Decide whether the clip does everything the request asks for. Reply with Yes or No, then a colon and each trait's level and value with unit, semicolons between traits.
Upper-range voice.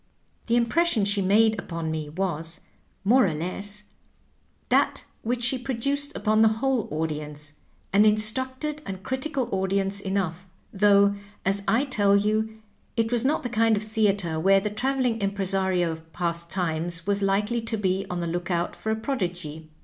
Yes: high, 200 Hz